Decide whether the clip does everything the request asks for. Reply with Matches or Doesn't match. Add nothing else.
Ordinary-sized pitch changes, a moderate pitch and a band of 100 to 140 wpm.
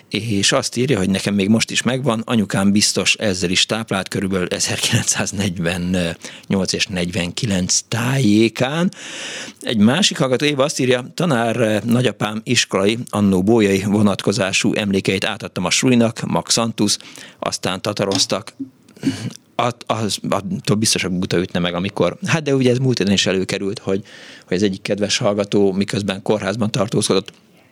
Doesn't match